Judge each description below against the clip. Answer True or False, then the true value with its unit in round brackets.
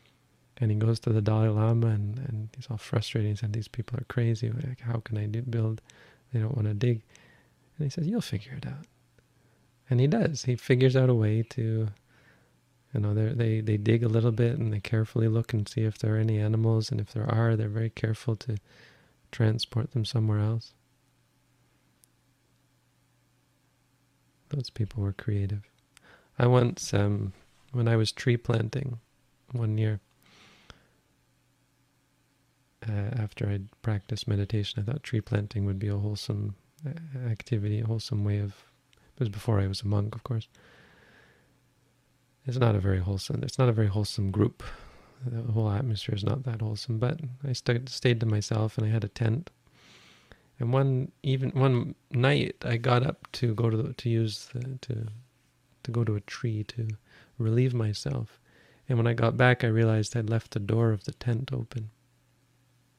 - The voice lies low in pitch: True (115 Hz)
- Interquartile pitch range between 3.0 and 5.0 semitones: False (2.5 semitones)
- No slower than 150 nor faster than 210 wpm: True (175 wpm)